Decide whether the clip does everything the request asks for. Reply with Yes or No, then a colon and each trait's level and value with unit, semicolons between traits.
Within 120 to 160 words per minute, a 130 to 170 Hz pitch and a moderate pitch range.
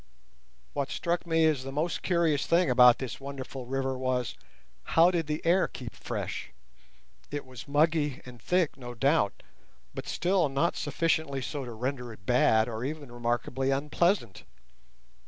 Yes: average, 155 wpm; medium, 140 Hz; average, 4.3 semitones